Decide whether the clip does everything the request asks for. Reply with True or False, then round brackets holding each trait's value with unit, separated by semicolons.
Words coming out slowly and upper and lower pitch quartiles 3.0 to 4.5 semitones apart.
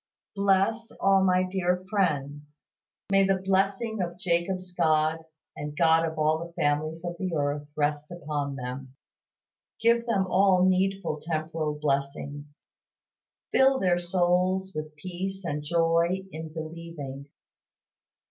True (125 wpm; 3.9 semitones)